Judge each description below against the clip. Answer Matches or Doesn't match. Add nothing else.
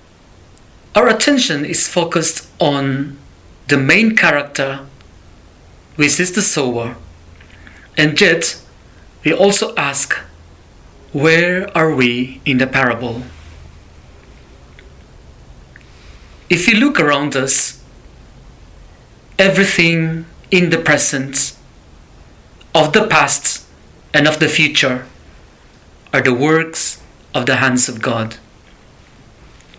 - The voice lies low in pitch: Matches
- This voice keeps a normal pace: Doesn't match